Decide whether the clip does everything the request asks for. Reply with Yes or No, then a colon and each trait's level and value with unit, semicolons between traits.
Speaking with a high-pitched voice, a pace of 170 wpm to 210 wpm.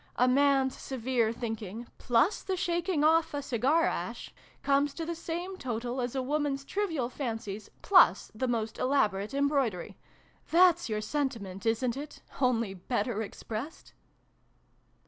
No: very high, 260 Hz; slow, 135 wpm